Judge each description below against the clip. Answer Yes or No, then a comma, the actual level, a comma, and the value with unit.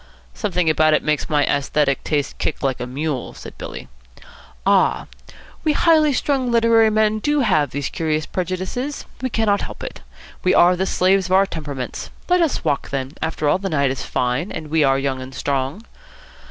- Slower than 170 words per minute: No, average, 185 wpm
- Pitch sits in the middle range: Yes, medium, 160 Hz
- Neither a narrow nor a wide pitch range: No, wide, 7.3 semitones